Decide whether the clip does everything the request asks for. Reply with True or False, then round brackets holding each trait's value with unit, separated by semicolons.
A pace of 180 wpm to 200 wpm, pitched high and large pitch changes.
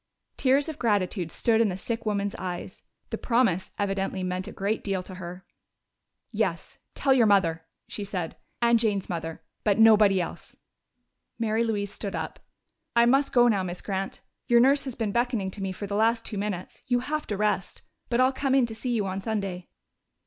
False (190 wpm; 210 Hz; 3.7 semitones)